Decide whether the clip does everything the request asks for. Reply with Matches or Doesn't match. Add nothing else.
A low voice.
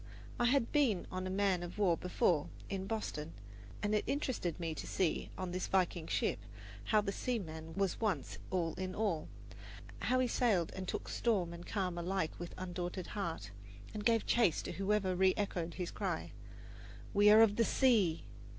Doesn't match